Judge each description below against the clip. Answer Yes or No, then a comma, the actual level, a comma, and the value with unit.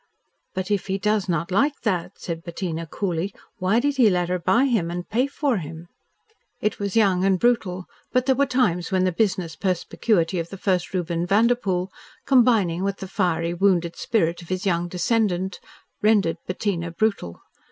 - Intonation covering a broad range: No, average, 3.8 semitones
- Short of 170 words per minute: No, average, 175 wpm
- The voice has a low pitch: No, medium, 185 Hz